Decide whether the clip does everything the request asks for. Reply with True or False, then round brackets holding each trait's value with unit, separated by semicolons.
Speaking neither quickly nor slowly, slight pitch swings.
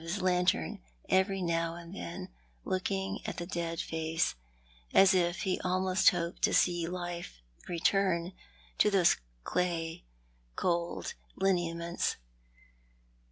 False (115 wpm; 1.8 semitones)